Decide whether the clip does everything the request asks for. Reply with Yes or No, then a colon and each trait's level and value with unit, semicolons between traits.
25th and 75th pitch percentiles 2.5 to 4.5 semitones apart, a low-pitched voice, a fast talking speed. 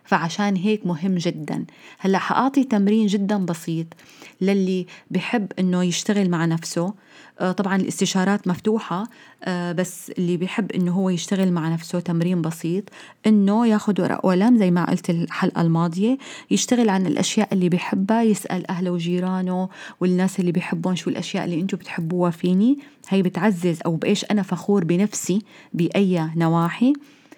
No: average, 2.9 semitones; medium, 185 Hz; fast, 140 wpm